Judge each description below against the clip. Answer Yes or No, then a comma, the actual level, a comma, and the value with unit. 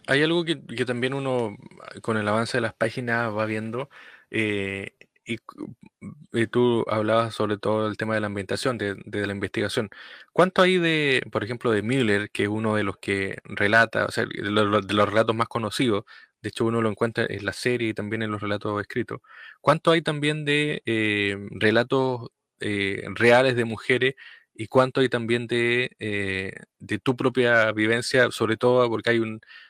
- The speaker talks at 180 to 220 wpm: Yes, average, 185 wpm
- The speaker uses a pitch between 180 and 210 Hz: No, low, 115 Hz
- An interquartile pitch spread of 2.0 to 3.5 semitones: Yes, average, 3.0 semitones